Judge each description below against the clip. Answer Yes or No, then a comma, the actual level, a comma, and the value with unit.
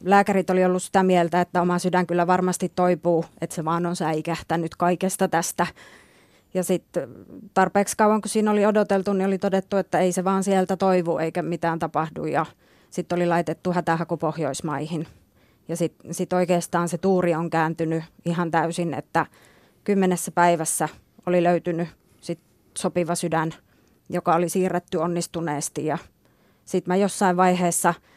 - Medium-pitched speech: Yes, medium, 175 Hz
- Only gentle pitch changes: Yes, narrow, 1.8 semitones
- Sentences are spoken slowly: No, average, 150 wpm